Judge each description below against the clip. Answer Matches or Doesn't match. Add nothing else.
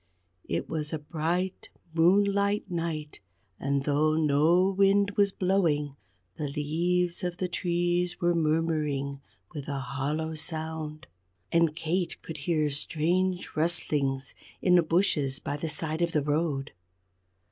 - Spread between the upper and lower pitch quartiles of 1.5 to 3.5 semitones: Matches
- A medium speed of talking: Doesn't match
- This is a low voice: Doesn't match